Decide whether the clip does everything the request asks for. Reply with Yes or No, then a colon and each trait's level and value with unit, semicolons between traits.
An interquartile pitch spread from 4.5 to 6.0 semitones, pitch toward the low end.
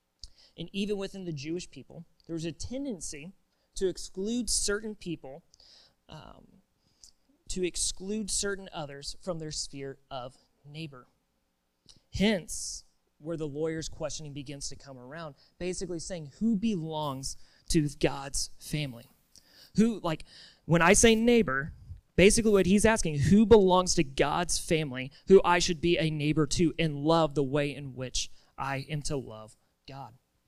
No: average, 5.0 semitones; medium, 160 Hz